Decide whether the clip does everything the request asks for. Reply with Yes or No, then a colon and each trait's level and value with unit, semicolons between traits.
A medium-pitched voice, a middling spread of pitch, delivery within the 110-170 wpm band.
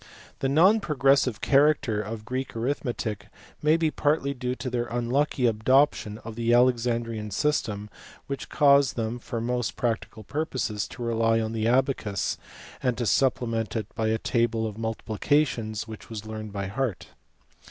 No: low, 120 Hz; average, 3.5 semitones; average, 160 wpm